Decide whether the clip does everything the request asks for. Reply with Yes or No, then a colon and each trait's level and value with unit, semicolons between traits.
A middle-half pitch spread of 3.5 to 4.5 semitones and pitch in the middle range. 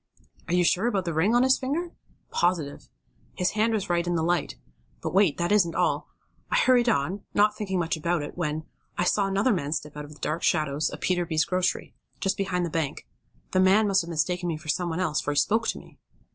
Yes: average, 3.9 semitones; medium, 175 Hz